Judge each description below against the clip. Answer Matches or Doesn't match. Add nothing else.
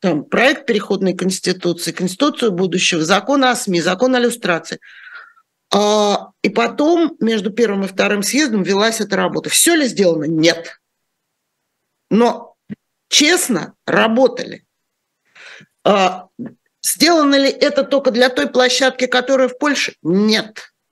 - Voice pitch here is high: Matches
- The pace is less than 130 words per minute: Matches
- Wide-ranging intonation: Matches